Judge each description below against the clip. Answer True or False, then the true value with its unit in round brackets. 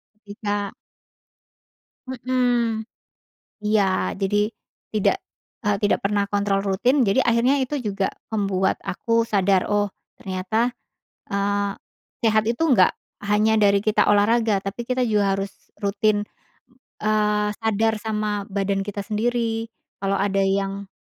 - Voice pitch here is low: False (210 Hz)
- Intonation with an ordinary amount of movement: False (2.1 semitones)